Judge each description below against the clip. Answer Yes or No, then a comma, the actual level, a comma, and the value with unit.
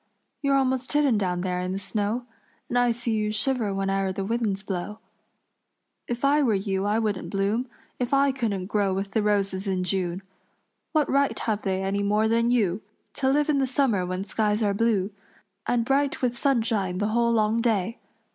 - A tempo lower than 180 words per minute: No, average, 190 wpm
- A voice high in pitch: Yes, high, 215 Hz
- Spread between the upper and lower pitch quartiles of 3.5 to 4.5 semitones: Yes, average, 3.8 semitones